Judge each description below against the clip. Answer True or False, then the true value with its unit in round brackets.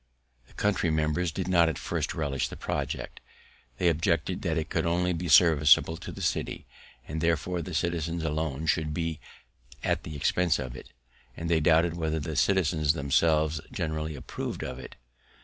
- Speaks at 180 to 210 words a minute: False (170 wpm)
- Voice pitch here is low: True (80 Hz)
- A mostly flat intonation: True (1.8 semitones)